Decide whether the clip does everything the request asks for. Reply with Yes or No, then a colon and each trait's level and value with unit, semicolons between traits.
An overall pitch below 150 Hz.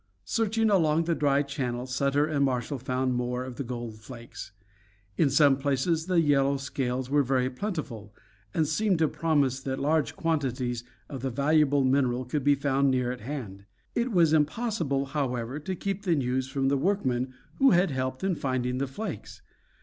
Yes: medium, 140 Hz